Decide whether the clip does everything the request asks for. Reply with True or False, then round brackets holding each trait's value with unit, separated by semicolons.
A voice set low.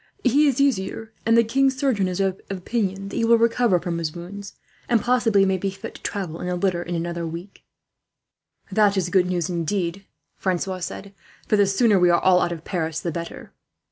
False (195 Hz)